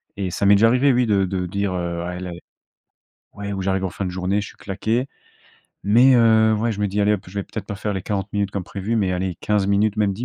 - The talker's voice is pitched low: Yes, low, 100 Hz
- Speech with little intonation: Yes, narrow, 2.2 semitones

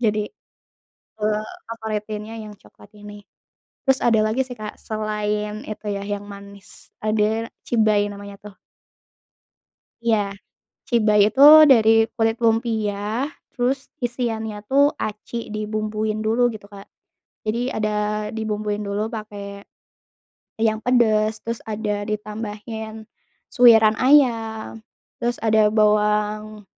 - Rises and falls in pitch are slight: Yes, narrow, 1.2 semitones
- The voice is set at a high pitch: Yes, high, 215 Hz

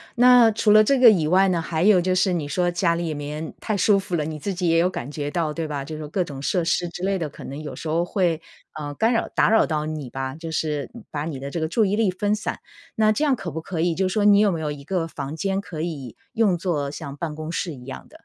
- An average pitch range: Yes, average, 4.3 semitones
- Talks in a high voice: No, medium, 170 Hz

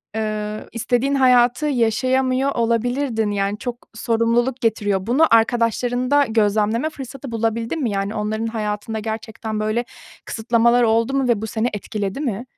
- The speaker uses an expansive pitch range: No, narrow, 2.4 semitones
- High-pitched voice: Yes, high, 230 Hz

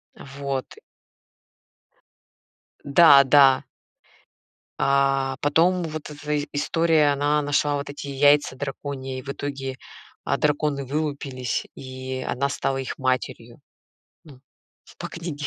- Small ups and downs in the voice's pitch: Yes, narrow, 1.7 semitones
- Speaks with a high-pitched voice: No, medium, 140 Hz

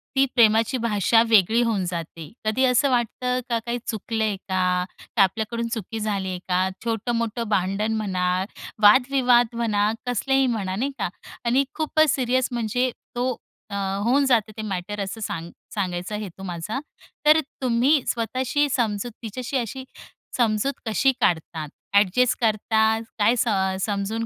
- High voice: Yes, high, 225 Hz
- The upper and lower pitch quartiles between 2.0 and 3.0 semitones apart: No, average, 3.8 semitones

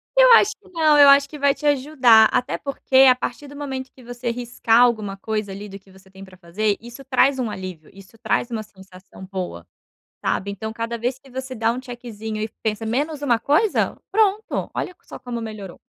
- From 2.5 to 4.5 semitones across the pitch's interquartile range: No, average, 4.9 semitones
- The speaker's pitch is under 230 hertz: No, high, 235 Hz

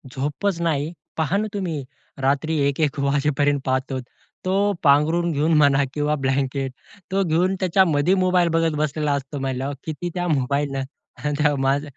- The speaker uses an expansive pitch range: No, average, 3.5 semitones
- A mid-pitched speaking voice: Yes, medium, 150 Hz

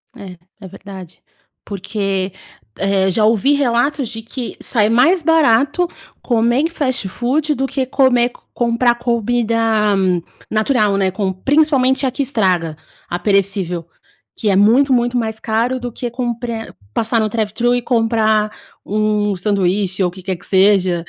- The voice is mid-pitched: No, high, 225 Hz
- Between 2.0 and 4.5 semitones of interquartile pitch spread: Yes, average, 4.0 semitones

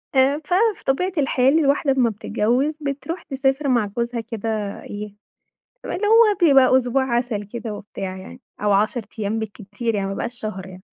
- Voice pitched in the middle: No, high, 245 Hz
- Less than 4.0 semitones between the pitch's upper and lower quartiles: No, average, 4.8 semitones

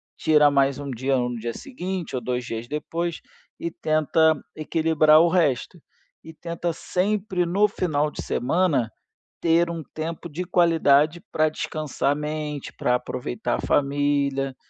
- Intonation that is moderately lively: Yes, average, 3.5 semitones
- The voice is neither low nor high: Yes, medium, 155 Hz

